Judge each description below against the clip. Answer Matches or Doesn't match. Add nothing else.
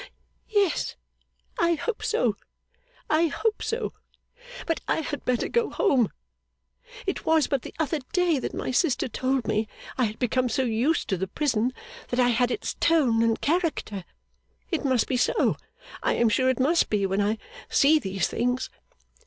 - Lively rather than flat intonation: Matches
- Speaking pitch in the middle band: Doesn't match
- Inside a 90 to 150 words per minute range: Doesn't match